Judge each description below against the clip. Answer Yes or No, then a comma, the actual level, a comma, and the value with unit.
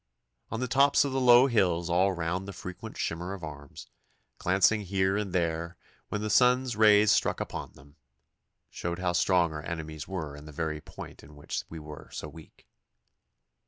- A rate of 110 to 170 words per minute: No, average, 180 wpm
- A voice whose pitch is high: No, very low, 90 Hz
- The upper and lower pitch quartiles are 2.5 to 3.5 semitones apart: No, average, 4.7 semitones